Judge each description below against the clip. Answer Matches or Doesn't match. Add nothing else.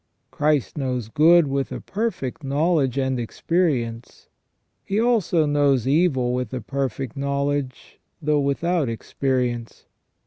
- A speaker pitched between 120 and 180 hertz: Matches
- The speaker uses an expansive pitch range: Doesn't match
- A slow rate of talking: Matches